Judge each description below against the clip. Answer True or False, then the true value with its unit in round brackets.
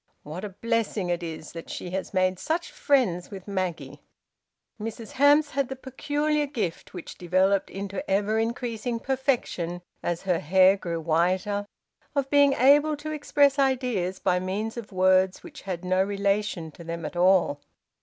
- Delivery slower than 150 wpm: False (155 wpm)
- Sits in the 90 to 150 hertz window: False (200 Hz)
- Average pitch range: False (6.3 semitones)